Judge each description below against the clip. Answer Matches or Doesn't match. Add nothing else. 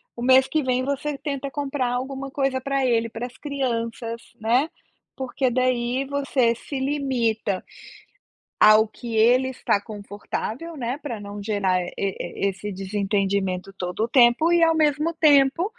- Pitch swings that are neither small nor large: Matches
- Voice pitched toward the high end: Matches